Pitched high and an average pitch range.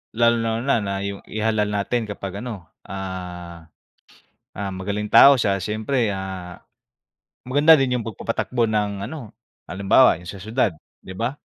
No: low, 105 Hz; average, 3.4 semitones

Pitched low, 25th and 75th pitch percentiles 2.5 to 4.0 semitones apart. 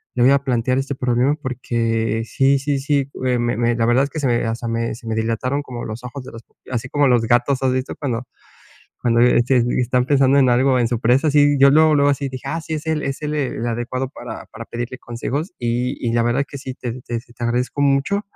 Yes: low, 125 Hz; average, 2.8 semitones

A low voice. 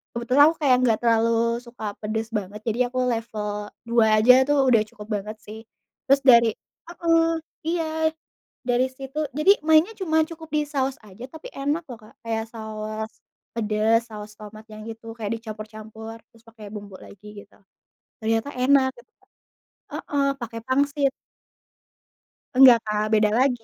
No: high, 235 Hz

